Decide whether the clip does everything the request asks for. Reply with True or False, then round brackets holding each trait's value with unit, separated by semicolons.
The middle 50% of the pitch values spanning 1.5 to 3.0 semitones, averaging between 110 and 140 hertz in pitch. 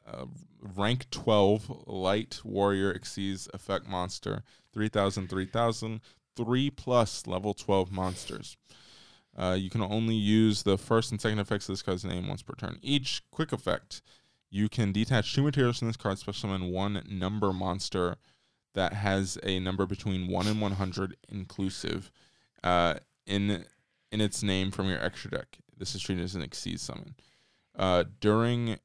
False (2.6 semitones; 100 Hz)